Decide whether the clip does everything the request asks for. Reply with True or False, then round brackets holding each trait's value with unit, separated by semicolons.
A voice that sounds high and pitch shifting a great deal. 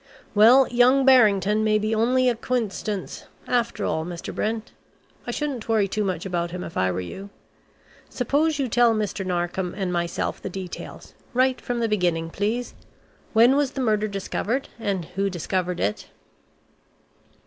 False (215 Hz; 4.9 semitones)